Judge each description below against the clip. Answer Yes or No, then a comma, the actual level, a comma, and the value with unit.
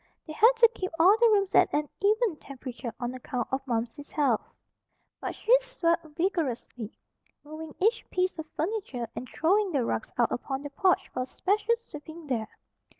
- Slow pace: No, average, 175 wpm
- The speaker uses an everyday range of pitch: No, wide, 7.5 semitones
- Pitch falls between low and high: No, very high, 315 Hz